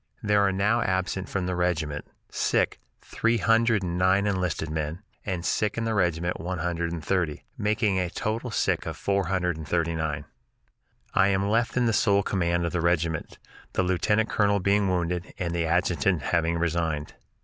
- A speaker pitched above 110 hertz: No, very low, 90 Hz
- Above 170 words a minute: Yes, average, 180 wpm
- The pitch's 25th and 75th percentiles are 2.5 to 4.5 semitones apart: Yes, average, 3.1 semitones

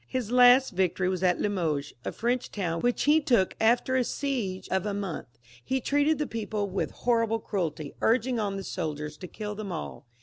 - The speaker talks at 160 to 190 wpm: No, fast, 205 wpm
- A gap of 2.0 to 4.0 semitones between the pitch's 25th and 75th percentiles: No, average, 5.2 semitones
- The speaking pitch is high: Yes, high, 210 Hz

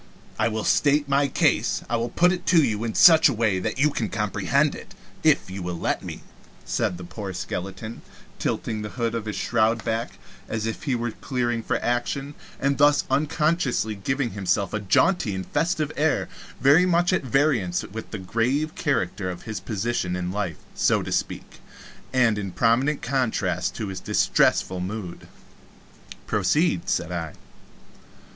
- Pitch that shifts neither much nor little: No, wide, 6.1 semitones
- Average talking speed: Yes, average, 170 wpm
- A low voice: Yes, low, 115 Hz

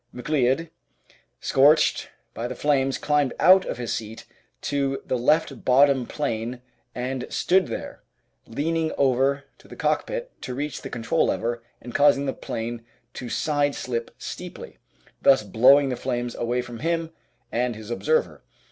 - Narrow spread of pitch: No, average, 3.4 semitones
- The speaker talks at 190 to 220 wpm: No, average, 145 wpm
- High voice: No, low, 135 Hz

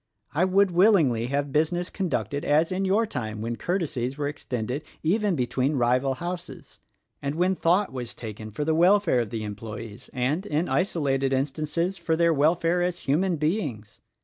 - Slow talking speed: No, average, 170 wpm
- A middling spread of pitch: No, wide, 5.8 semitones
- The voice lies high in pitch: No, medium, 150 Hz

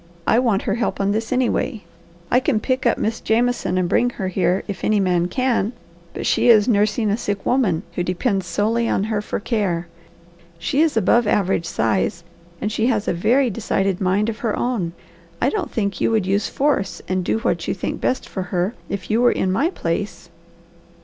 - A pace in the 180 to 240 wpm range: Yes, fast, 205 wpm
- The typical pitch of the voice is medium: No, high, 210 Hz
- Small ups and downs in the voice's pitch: No, average, 4.0 semitones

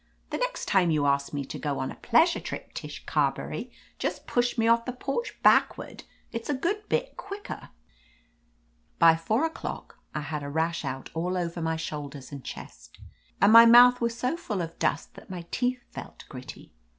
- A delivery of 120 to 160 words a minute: No, average, 185 wpm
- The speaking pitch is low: No, medium, 185 Hz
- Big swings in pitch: Yes, wide, 8.4 semitones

